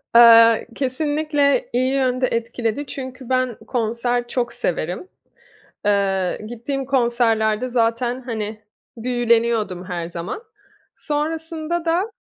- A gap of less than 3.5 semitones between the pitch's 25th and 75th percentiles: Yes, average, 3.1 semitones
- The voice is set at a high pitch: Yes, high, 240 Hz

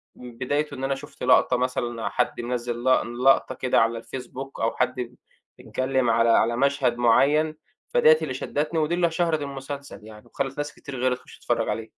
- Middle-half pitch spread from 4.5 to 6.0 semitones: No, average, 3.2 semitones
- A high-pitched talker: No, low, 130 Hz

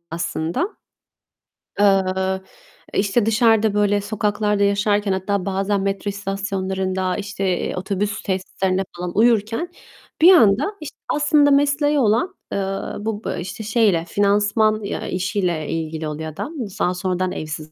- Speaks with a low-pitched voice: No, high, 200 Hz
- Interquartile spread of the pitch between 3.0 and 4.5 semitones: No, narrow, 2.6 semitones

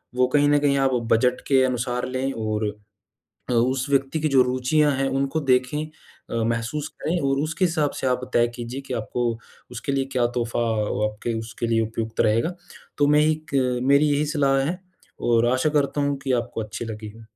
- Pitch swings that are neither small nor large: Yes, average, 3.5 semitones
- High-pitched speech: No, low, 130 Hz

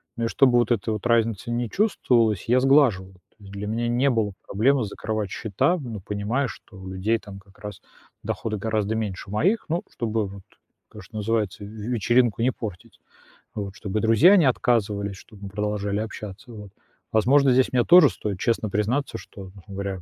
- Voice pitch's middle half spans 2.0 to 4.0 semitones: Yes, average, 3.1 semitones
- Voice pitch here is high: No, low, 110 Hz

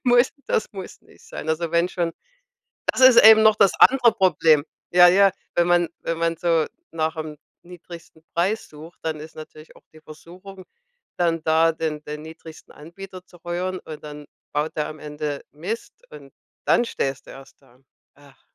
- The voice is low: No, medium, 165 Hz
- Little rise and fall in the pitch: No, average, 3.0 semitones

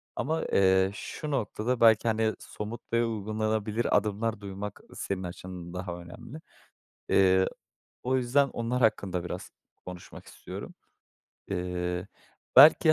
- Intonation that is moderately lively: Yes, average, 3.9 semitones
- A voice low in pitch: Yes, low, 105 Hz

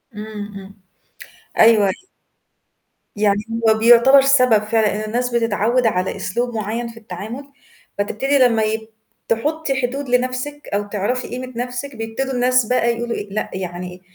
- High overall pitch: Yes, high, 230 Hz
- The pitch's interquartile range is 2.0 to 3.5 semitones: Yes, average, 3.2 semitones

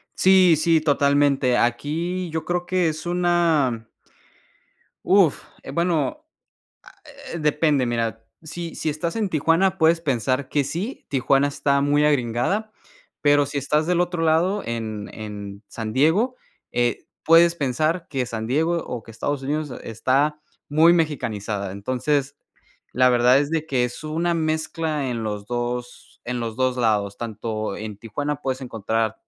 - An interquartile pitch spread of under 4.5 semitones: No, wide, 5.4 semitones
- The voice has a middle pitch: Yes, medium, 145 Hz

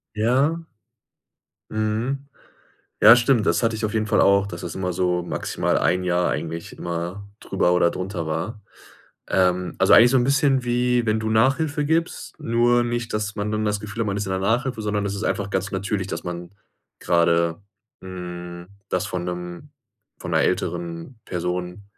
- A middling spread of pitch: Yes, average, 4.6 semitones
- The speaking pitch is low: Yes, low, 100 Hz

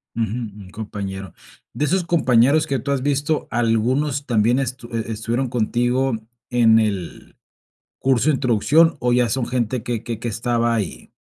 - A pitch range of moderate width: Yes, average, 3.1 semitones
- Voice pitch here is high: No, low, 120 Hz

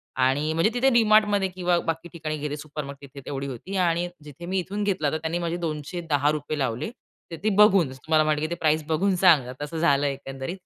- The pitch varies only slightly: No, average, 3.8 semitones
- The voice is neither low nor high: Yes, medium, 160 Hz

